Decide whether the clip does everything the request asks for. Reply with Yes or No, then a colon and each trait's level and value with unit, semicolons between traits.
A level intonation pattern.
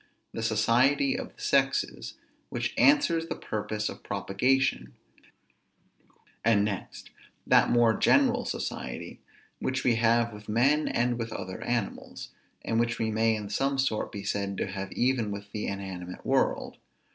No: average, 4.1 semitones